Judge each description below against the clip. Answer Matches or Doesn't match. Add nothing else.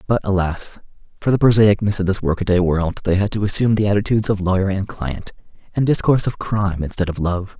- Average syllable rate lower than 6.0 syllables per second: Doesn't match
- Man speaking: Matches